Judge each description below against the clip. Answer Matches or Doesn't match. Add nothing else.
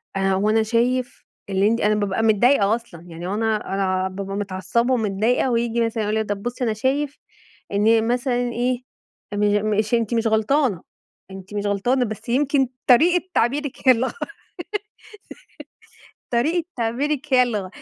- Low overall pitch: Doesn't match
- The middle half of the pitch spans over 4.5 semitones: Doesn't match